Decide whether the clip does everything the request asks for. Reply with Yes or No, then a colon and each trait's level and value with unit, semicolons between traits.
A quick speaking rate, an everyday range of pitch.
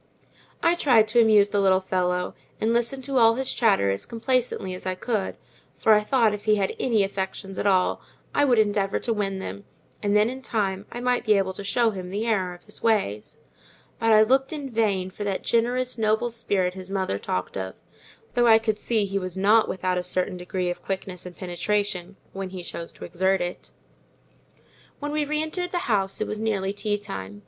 Yes: fast, 210 wpm; average, 3.4 semitones